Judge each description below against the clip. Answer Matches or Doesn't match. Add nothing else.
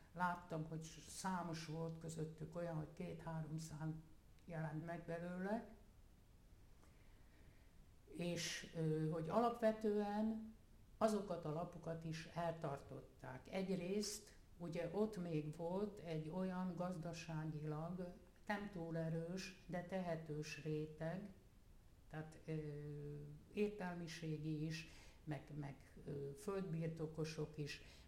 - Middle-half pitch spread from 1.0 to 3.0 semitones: Matches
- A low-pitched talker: Doesn't match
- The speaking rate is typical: Doesn't match